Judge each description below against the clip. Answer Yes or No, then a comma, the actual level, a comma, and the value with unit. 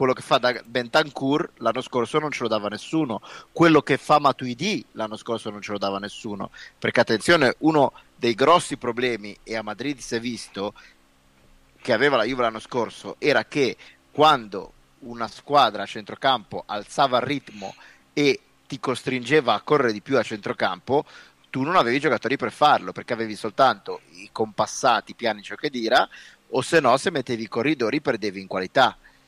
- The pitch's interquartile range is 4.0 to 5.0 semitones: Yes, average, 4.6 semitones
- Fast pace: Yes, fast, 175 wpm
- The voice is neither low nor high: No, low, 120 Hz